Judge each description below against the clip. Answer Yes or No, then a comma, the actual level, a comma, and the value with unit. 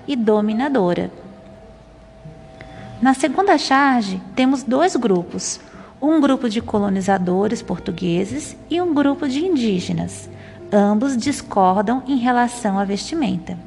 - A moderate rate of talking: No, slow, 105 wpm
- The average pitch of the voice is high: Yes, high, 235 Hz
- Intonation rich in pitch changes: Yes, wide, 6.0 semitones